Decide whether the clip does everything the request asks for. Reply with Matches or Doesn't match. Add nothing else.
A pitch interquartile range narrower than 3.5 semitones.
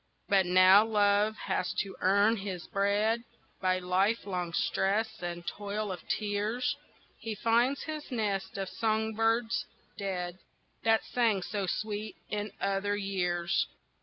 Matches